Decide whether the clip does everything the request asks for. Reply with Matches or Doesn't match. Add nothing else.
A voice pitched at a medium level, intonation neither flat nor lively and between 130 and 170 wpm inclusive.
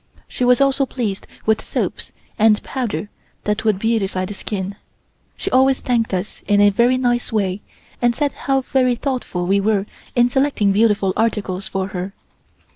Doesn't match